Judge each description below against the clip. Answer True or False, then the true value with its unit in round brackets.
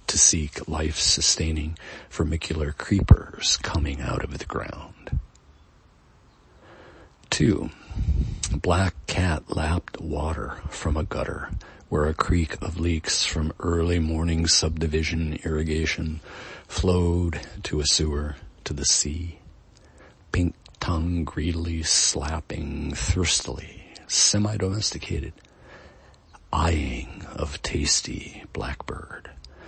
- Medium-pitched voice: False (80 Hz)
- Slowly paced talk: True (90 wpm)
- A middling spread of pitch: False (2.3 semitones)